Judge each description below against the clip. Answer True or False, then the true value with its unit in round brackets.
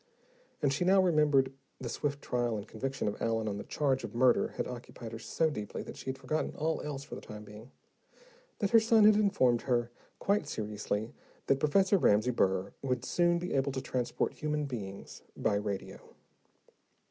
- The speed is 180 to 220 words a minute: True (185 wpm)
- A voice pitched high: False (130 Hz)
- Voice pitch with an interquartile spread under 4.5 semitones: False (5.3 semitones)